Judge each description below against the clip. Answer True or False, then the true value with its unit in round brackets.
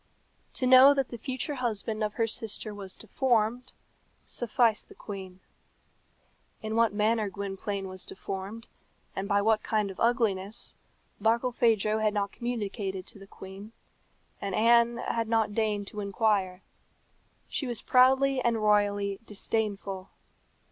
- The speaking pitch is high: True (215 Hz)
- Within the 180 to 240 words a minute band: False (135 wpm)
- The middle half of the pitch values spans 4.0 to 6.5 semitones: False (2.7 semitones)